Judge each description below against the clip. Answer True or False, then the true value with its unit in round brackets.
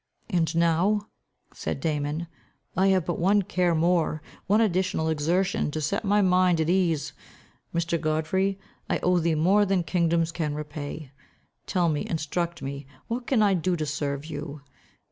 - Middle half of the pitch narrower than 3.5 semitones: True (3.1 semitones)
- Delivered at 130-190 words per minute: True (160 wpm)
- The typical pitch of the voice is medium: True (170 Hz)